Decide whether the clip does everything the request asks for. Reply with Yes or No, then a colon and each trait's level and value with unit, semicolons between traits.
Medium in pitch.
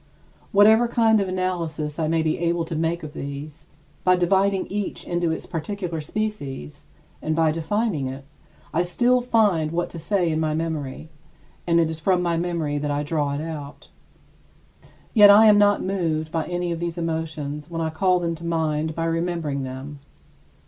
Yes: medium, 165 Hz